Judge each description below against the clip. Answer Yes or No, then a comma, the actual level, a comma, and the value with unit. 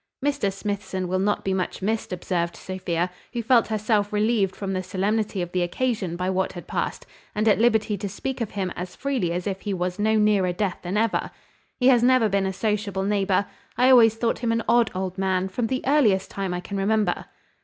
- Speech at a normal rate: No, fast, 215 wpm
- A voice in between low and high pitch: No, high, 200 Hz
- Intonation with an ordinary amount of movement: Yes, average, 3.1 semitones